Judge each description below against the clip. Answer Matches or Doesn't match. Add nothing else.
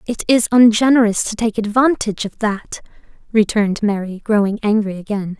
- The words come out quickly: Doesn't match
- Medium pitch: Doesn't match